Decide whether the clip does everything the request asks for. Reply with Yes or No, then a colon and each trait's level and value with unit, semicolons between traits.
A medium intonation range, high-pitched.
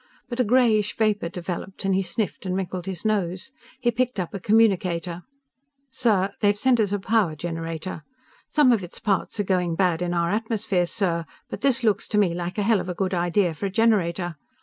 Yes: average, 3.6 semitones; high, 195 Hz